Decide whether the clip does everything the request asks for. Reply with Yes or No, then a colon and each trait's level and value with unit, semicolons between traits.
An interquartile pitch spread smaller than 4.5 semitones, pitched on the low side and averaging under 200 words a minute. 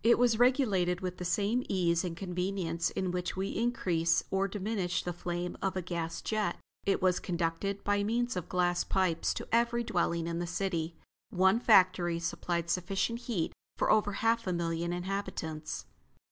No: average, 2.9 semitones; medium, 185 Hz; average, 170 wpm